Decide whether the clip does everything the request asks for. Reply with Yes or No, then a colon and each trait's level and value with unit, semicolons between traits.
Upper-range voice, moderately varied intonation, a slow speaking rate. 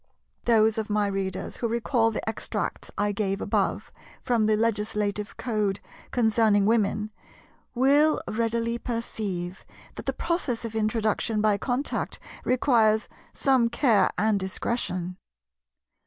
No: high, 220 Hz; narrow, 2.2 semitones; slow, 120 wpm